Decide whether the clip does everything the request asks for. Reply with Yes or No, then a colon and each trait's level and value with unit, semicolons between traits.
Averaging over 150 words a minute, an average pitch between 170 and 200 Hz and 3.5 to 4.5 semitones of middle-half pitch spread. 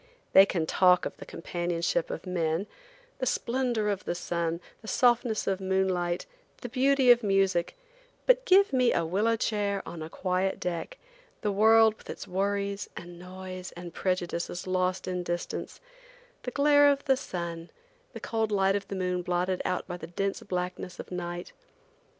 Yes: average, 170 wpm; high, 190 Hz; average, 3.9 semitones